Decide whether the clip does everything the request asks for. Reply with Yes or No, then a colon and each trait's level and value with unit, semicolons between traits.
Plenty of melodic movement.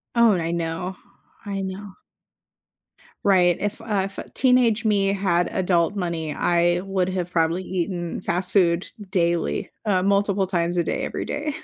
No: narrow, 2.6 semitones